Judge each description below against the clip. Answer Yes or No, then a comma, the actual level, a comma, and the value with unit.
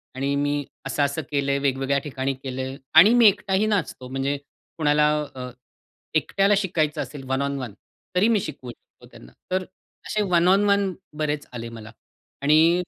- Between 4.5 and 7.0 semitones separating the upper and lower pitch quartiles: Yes, average, 5.2 semitones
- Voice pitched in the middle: Yes, medium, 145 Hz